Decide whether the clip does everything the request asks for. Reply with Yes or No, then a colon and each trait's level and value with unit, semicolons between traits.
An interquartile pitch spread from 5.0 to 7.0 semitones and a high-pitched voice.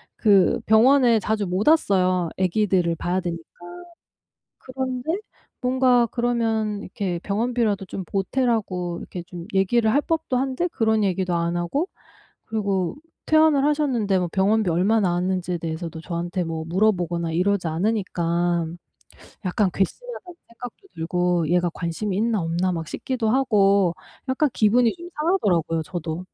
Yes: average, 5.3 semitones; high, 195 Hz